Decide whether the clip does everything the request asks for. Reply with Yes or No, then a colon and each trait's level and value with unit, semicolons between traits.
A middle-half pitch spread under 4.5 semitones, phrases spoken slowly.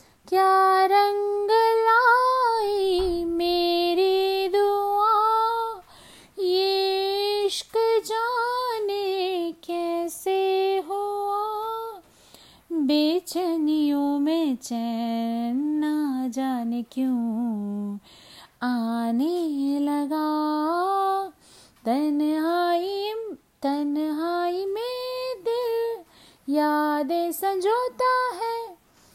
No: wide, 5.4 semitones; slow, 50 wpm